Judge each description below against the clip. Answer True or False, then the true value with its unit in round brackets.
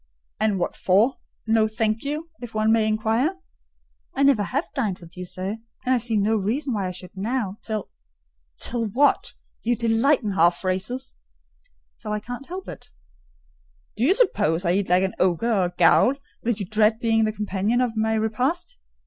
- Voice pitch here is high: True (220 Hz)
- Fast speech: False (185 wpm)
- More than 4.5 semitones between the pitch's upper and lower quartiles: False (3.7 semitones)